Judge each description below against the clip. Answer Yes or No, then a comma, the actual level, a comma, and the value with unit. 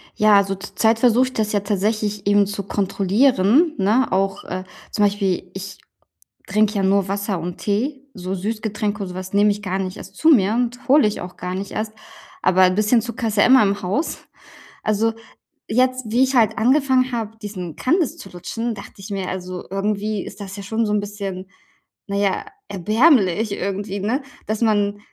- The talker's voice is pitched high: Yes, high, 205 Hz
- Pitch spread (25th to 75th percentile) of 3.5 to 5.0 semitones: No, average, 2.7 semitones